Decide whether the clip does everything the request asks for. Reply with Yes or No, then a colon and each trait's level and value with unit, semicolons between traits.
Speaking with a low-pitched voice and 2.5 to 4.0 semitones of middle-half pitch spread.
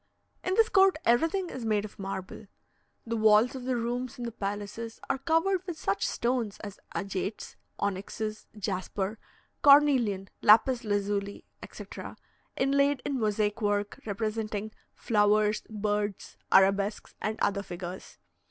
No: high, 215 Hz; average, 3.5 semitones